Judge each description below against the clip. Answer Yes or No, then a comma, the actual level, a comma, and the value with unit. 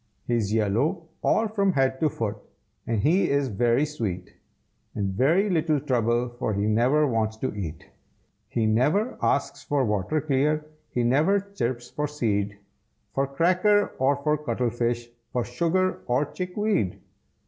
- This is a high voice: No, low, 130 Hz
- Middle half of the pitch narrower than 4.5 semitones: No, wide, 5.5 semitones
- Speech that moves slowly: No, average, 145 wpm